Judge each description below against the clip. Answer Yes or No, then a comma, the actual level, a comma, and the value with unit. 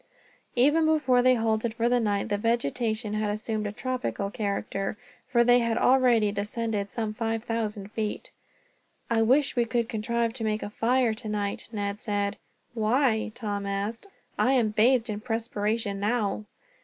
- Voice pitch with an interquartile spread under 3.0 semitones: Yes, narrow, 2.4 semitones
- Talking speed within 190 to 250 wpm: No, average, 155 wpm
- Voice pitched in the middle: No, high, 225 Hz